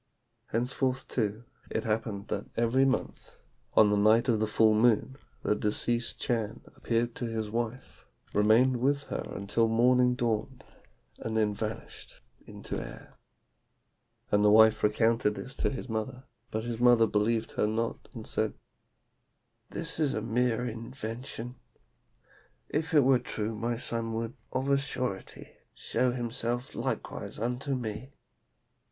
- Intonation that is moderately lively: No, narrow, 2.3 semitones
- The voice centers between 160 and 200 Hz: No, low, 115 Hz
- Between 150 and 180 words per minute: No, average, 140 wpm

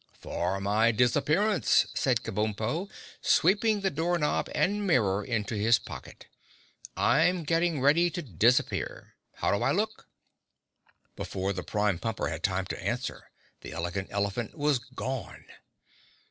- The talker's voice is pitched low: Yes, low, 120 Hz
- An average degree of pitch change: No, wide, 8.6 semitones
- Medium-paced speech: No, slow, 130 wpm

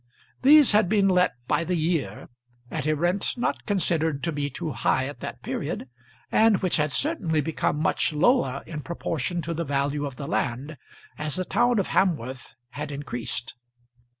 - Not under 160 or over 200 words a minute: Yes, average, 175 wpm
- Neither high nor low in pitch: Yes, medium, 160 Hz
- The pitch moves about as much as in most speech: Yes, average, 4.4 semitones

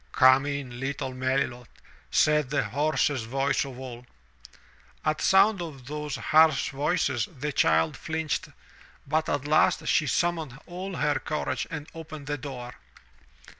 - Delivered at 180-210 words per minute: No, slow, 135 wpm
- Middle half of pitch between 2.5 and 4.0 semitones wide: Yes, average, 3.1 semitones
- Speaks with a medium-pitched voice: Yes, medium, 145 Hz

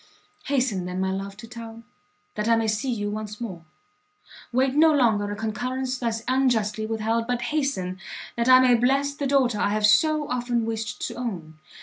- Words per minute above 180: Yes, average, 190 wpm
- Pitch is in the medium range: No, high, 230 Hz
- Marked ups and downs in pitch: No, average, 3.5 semitones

